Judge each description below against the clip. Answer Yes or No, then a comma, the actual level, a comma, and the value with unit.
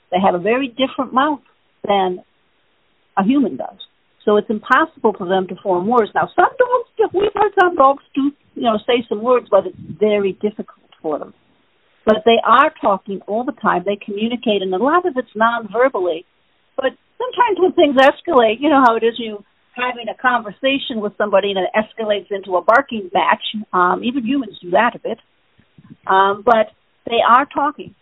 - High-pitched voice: Yes, high, 230 Hz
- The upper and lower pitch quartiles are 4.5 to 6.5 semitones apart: Yes, average, 4.8 semitones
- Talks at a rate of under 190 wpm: Yes, average, 180 wpm